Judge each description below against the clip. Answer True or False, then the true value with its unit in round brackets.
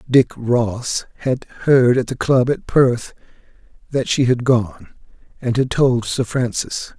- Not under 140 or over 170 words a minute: True (155 wpm)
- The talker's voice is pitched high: False (125 Hz)